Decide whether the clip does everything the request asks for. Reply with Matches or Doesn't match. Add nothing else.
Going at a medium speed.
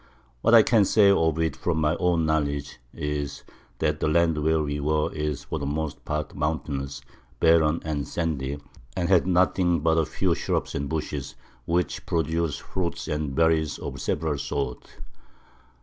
Matches